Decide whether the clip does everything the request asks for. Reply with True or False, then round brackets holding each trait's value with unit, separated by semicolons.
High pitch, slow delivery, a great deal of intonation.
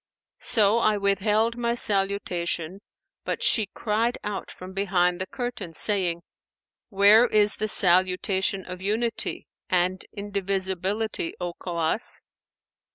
False (195 Hz; 110 wpm; 2.7 semitones)